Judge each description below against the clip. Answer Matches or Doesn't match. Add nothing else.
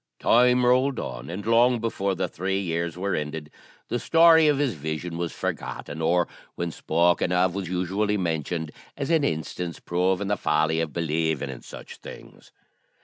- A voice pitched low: Matches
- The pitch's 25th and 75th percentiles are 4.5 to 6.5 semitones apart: Matches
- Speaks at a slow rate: Doesn't match